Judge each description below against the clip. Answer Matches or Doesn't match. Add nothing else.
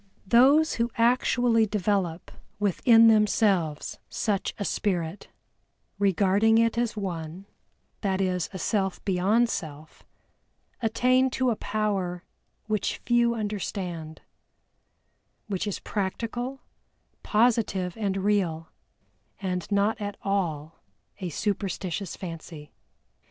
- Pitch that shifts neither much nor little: Matches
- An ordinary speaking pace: Doesn't match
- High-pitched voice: Matches